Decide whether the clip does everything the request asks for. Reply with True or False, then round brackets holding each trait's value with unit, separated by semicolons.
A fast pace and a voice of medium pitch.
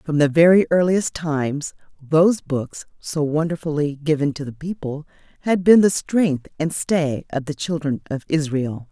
False (160 wpm; 155 Hz)